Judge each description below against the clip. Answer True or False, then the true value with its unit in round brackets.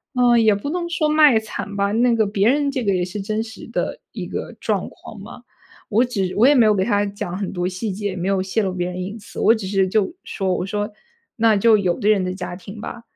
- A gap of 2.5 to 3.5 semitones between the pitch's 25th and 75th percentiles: True (3.2 semitones)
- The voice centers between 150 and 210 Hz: True (205 Hz)